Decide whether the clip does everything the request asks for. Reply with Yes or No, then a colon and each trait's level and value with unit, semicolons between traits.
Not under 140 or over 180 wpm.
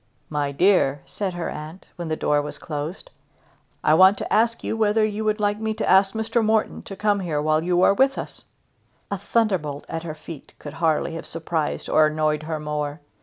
No: fast, 205 wpm